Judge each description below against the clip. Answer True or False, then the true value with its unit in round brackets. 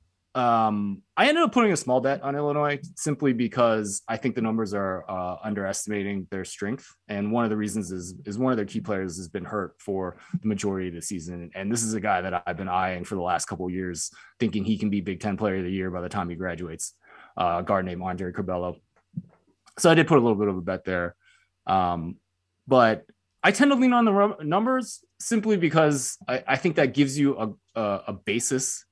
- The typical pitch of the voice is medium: False (105 Hz)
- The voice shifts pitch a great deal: True (6.9 semitones)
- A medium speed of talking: False (225 wpm)